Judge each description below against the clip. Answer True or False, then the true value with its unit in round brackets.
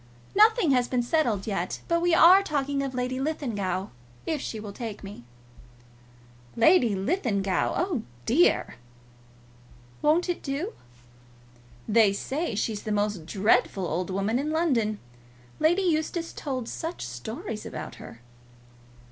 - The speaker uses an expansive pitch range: True (7.6 semitones)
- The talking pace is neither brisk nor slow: False (130 wpm)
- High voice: True (250 Hz)